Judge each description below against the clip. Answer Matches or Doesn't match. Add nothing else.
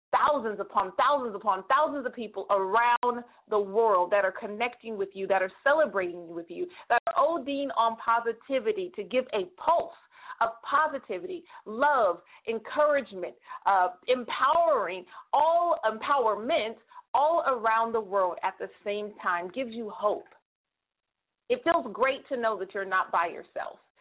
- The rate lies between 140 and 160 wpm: Matches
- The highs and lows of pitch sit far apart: Matches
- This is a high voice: Matches